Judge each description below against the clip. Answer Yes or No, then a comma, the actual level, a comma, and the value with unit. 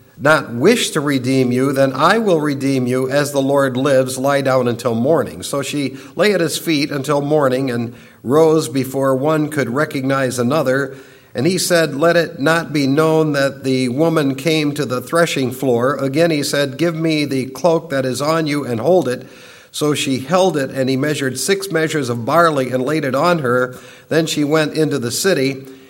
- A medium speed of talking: Yes, average, 195 wpm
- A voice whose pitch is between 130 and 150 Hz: Yes, medium, 140 Hz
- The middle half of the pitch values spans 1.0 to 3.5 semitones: Yes, average, 3.2 semitones